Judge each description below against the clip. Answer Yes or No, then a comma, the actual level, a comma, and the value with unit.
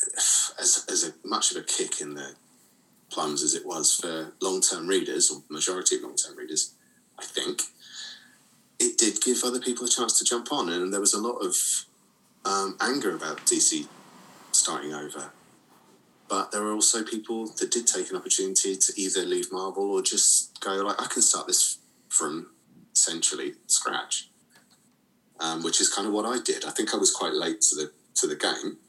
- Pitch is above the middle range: Yes, very high, 365 Hz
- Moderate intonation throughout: Yes, average, 3.5 semitones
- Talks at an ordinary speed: Yes, average, 185 wpm